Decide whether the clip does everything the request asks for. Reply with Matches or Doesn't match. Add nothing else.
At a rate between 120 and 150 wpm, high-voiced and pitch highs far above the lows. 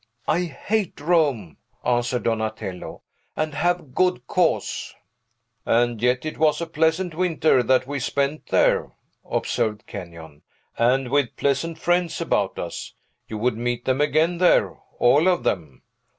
Doesn't match